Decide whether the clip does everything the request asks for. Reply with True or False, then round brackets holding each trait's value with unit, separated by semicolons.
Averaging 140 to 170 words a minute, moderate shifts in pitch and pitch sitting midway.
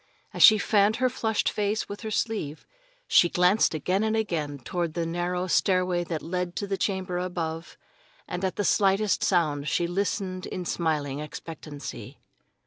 True (160 wpm; 3.5 semitones; 180 Hz)